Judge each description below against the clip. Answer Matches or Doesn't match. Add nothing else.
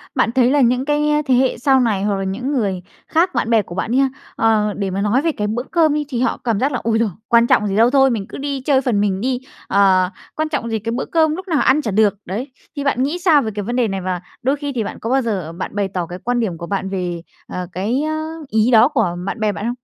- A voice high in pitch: Matches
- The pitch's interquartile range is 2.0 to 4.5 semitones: Doesn't match